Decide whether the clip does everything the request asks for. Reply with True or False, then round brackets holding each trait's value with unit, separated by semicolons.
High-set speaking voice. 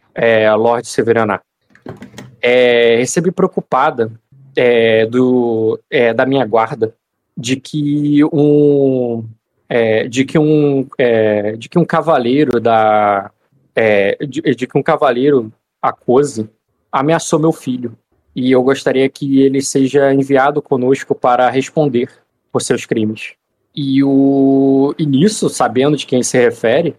False (130 Hz)